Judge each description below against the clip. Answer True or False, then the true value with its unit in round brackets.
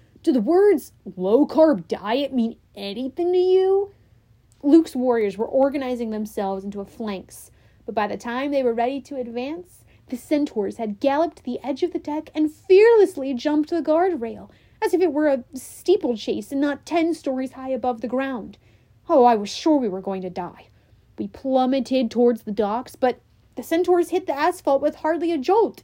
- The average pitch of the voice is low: False (265 Hz)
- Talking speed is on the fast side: False (185 wpm)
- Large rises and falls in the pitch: True (5.8 semitones)